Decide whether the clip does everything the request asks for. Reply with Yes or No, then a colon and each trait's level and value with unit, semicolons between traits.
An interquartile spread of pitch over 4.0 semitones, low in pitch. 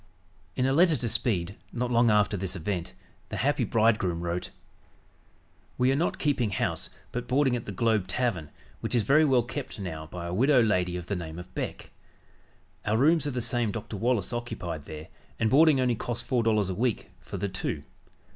Yes: average, 5.3 semitones; low, 110 Hz